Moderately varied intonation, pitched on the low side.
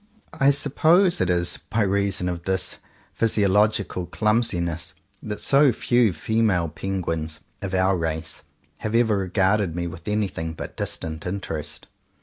Yes: average, 4.0 semitones; very low, 95 Hz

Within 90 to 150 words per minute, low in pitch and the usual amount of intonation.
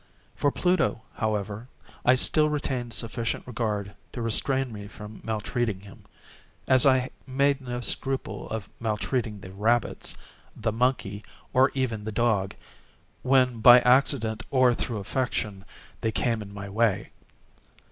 Yes: slow, 135 wpm; low, 115 Hz; average, 3.4 semitones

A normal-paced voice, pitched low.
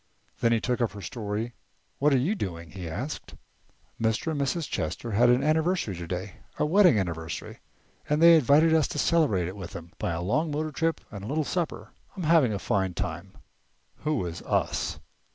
Yes: average, 190 wpm; low, 120 Hz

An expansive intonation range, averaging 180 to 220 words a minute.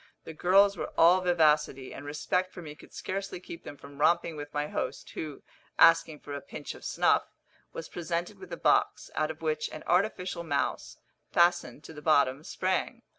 No: average, 3.2 semitones; average, 185 wpm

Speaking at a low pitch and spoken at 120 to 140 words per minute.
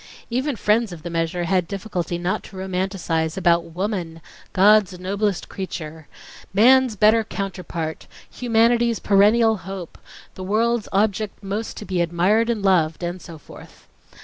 No: high, 190 Hz; slow, 135 wpm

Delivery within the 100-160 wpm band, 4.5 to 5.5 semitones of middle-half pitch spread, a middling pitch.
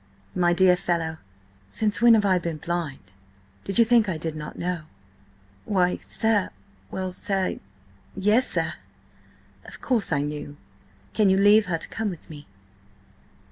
Yes: average, 140 wpm; average, 4.9 semitones; medium, 180 Hz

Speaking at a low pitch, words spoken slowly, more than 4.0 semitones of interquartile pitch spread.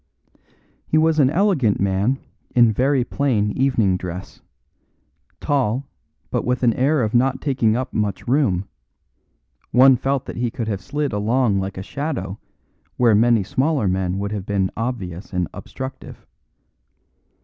No: low, 120 Hz; average, 145 wpm; average, 5.1 semitones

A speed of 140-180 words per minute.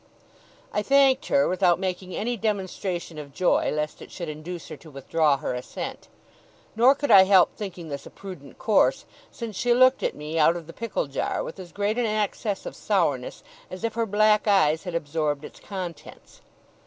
No: average, 190 wpm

